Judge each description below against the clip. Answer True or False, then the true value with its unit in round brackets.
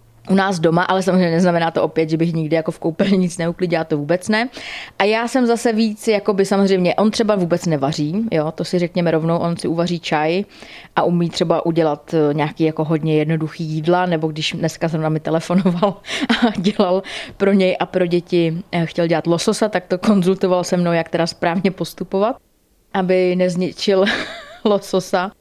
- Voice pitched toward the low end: False (180 Hz)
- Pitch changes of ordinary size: True (3.1 semitones)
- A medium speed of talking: False (185 wpm)